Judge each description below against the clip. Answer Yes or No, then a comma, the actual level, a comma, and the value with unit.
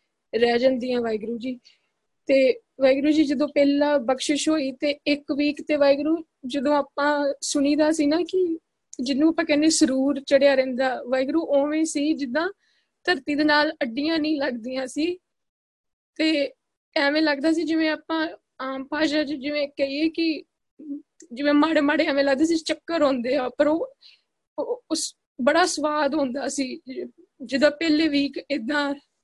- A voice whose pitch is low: No, very high, 295 Hz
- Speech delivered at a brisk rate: No, average, 145 wpm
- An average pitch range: No, narrow, 2.1 semitones